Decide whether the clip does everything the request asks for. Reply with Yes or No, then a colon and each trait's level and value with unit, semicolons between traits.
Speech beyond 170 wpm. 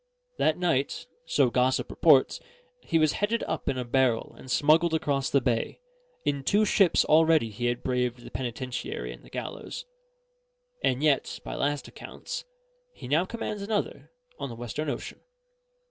No: average, 160 wpm